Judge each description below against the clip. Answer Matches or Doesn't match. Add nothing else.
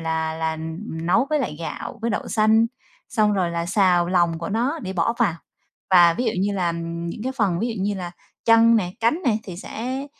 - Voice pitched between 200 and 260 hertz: Doesn't match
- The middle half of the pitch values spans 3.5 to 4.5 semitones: Doesn't match